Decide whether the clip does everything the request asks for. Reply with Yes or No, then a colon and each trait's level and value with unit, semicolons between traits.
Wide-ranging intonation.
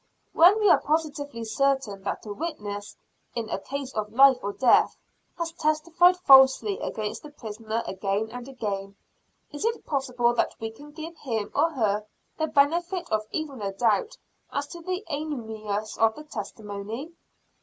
Yes: wide, 6.2 semitones